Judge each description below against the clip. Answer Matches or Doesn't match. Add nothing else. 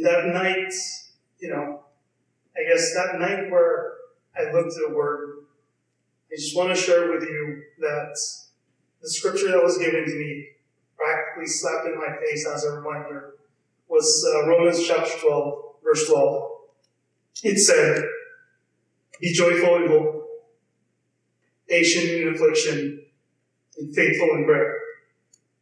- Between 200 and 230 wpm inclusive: Doesn't match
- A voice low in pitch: Doesn't match